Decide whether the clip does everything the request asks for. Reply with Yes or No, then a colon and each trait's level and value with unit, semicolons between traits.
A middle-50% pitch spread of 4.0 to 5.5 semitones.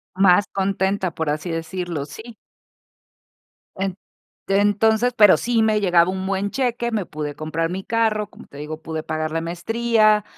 Yes: average, 4.6 semitones